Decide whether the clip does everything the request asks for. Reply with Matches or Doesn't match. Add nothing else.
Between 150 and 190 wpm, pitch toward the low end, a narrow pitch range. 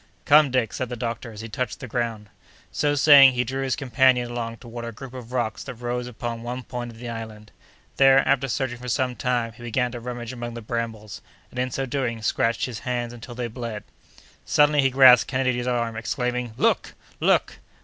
Doesn't match